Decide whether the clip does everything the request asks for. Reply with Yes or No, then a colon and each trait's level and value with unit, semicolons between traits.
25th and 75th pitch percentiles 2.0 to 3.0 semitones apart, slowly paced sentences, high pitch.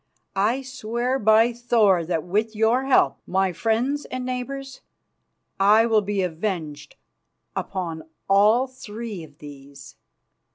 No: average, 5.3 semitones; slow, 120 wpm; high, 215 Hz